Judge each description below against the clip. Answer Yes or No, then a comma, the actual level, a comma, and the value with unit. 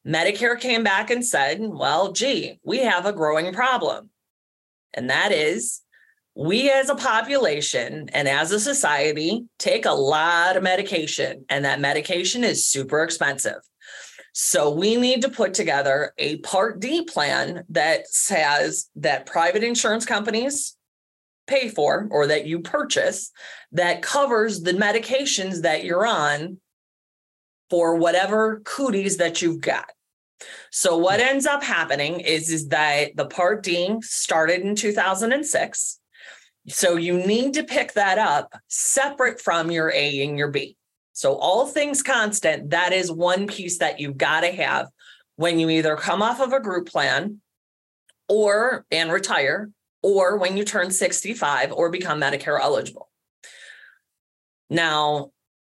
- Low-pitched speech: No, medium, 185 Hz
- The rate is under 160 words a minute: Yes, average, 140 wpm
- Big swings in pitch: Yes, wide, 6.4 semitones